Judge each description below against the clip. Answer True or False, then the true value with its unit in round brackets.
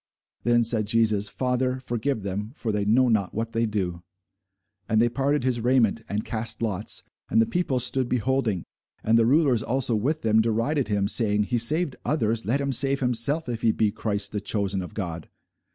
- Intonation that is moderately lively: True (3.3 semitones)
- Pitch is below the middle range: True (115 Hz)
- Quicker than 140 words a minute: True (190 wpm)